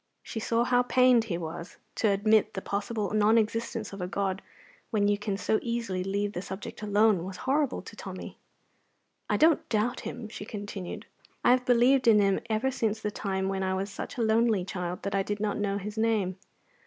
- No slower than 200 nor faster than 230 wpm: Yes, fast, 205 wpm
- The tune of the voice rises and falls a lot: No, average, 2.8 semitones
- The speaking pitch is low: No, high, 210 Hz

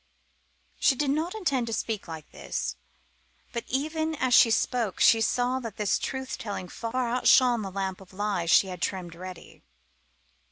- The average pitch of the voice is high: Yes, high, 230 Hz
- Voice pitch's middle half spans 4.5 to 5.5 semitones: Yes, average, 5.2 semitones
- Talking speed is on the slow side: No, average, 165 wpm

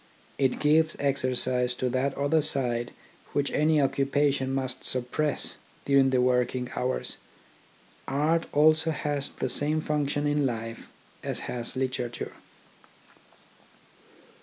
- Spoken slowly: Yes, slow, 110 wpm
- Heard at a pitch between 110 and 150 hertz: Yes, low, 135 Hz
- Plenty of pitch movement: No, narrow, 2.6 semitones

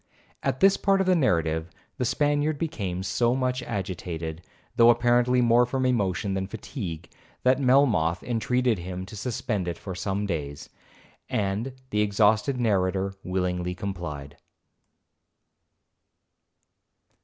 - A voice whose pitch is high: No, low, 105 Hz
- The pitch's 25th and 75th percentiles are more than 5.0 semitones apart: Yes, wide, 5.6 semitones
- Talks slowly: Yes, slow, 120 wpm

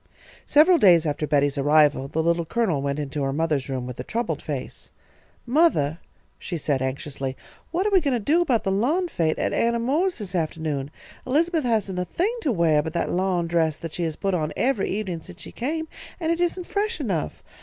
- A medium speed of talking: No, fast, 210 wpm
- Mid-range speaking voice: Yes, medium, 180 Hz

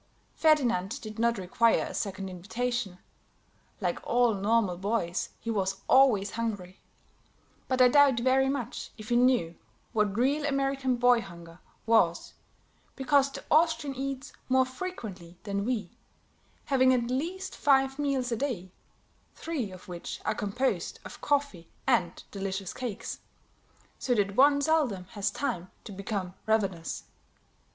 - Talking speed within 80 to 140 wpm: Yes, slow, 135 wpm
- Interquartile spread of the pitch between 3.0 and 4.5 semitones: No, wide, 5.5 semitones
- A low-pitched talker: No, high, 235 Hz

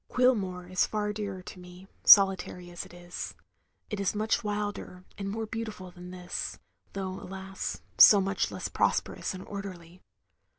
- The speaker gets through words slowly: No, average, 155 wpm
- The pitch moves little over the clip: Yes, narrow, 2.3 semitones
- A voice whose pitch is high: Yes, high, 195 Hz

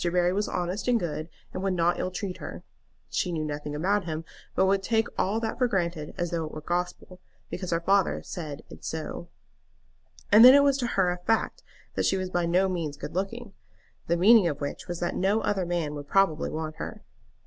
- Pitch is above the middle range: No, medium, 180 Hz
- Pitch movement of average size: Yes, average, 3.1 semitones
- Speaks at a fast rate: Yes, fast, 215 wpm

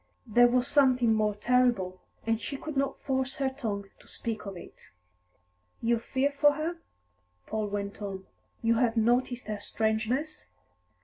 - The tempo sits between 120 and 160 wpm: Yes, average, 150 wpm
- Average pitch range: Yes, average, 3.7 semitones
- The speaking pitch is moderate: No, high, 235 Hz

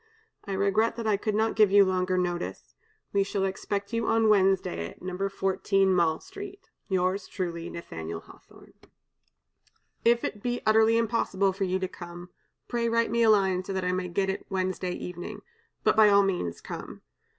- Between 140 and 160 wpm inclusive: No, average, 180 wpm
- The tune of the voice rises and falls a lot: No, average, 2.9 semitones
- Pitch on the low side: No, high, 195 Hz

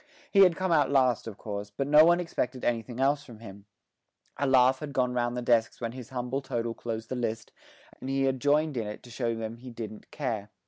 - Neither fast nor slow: No, fast, 230 wpm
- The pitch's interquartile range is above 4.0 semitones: No, average, 3.2 semitones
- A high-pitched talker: No, low, 125 Hz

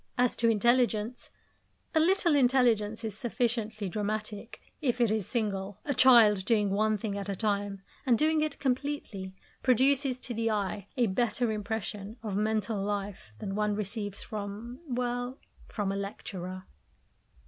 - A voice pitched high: Yes, high, 215 Hz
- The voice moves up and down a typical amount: Yes, average, 3.3 semitones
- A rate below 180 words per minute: Yes, average, 150 wpm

